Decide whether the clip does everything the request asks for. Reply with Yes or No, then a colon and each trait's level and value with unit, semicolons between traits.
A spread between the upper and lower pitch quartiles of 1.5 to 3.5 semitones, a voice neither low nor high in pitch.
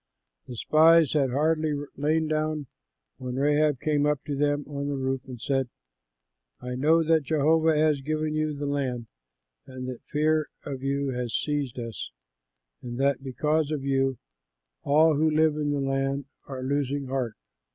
Yes: narrow, 2.4 semitones; medium, 145 Hz